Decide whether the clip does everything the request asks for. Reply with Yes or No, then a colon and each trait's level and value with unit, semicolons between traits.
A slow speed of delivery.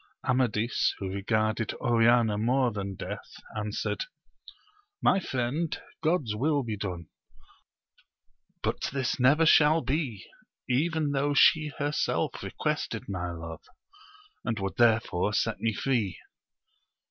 Yes: slow, 120 wpm